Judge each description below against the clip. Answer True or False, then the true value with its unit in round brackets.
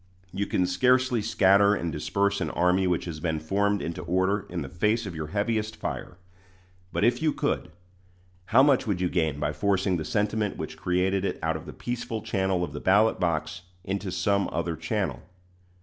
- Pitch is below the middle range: True (95 Hz)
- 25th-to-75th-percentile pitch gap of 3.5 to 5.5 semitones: False (3.1 semitones)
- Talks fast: False (190 wpm)